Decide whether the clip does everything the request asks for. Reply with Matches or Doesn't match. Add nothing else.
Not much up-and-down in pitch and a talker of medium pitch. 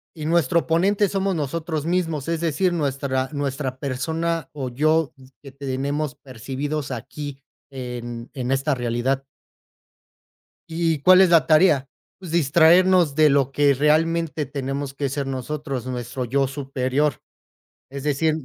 Doesn't match